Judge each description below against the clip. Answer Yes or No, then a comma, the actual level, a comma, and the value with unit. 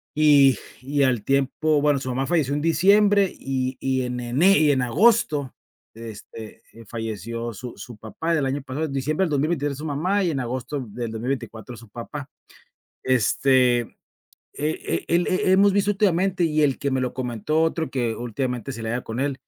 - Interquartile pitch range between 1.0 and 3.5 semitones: No, average, 4.2 semitones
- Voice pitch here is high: No, low, 135 Hz